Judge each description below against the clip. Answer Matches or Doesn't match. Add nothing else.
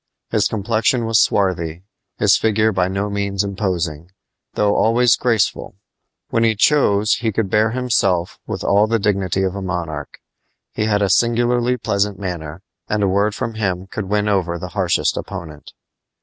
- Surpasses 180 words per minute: Doesn't match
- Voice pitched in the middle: Doesn't match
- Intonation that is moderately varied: Matches